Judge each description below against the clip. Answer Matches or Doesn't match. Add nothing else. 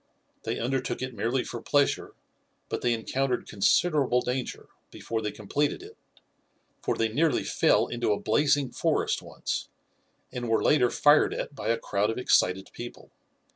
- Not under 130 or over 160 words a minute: Matches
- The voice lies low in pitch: Matches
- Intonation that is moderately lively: Matches